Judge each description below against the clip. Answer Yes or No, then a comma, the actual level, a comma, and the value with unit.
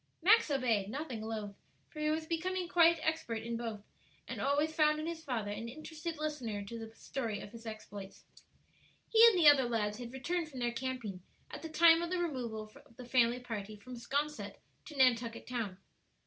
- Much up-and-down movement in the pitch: Yes, wide, 5.7 semitones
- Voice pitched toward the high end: Yes, very high, 255 Hz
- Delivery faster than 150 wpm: Yes, average, 190 wpm